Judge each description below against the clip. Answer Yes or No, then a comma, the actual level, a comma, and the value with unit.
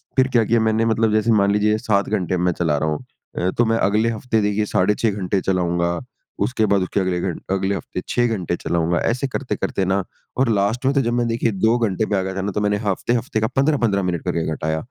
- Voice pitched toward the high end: No, low, 105 Hz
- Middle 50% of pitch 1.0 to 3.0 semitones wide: No, average, 3.6 semitones